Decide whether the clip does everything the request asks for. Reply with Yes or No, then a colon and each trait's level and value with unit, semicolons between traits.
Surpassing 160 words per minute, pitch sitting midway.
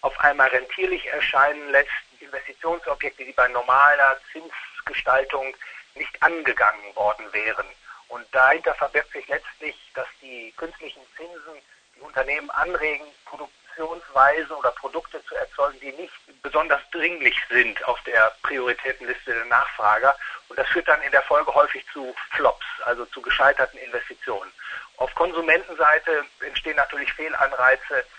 No: average, 130 wpm; medium, 145 Hz